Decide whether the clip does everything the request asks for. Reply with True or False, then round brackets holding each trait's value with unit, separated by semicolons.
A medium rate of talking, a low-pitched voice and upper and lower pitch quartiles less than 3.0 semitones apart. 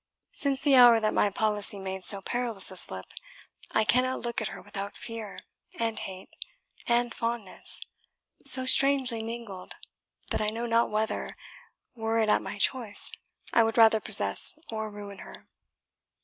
False (155 wpm; 225 Hz; 2.6 semitones)